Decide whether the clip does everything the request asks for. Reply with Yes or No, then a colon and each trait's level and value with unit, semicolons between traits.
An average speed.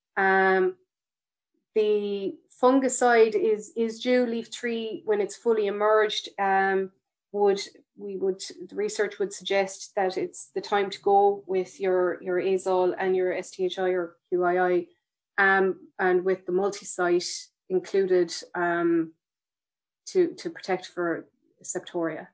No: slow, 125 wpm